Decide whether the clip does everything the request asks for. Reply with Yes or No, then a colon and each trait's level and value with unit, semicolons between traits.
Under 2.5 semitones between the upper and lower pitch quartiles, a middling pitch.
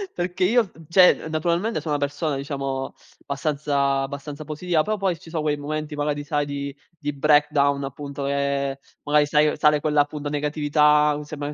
Yes: narrow, 1.5 semitones; medium, 150 Hz